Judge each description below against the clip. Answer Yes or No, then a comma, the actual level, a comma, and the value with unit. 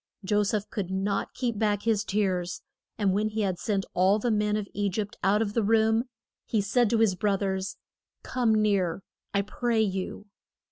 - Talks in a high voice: Yes, high, 205 Hz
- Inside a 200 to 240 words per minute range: No, average, 190 wpm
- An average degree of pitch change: No, narrow, 2.0 semitones